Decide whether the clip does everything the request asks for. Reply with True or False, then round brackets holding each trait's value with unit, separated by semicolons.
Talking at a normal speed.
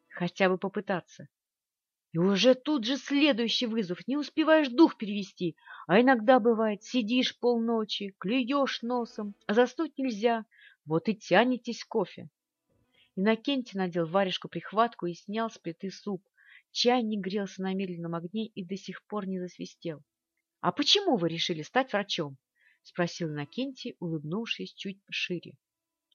True (135 wpm)